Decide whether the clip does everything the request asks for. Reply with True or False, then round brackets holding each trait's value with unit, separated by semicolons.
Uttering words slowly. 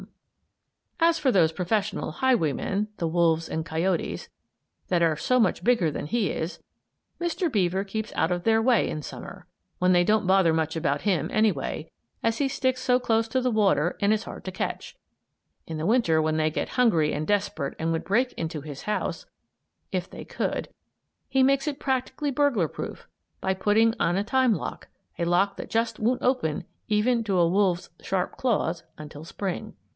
False (185 wpm)